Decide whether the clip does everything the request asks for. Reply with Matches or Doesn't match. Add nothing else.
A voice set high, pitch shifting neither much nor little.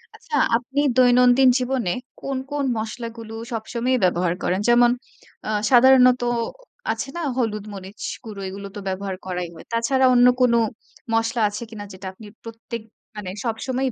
Matches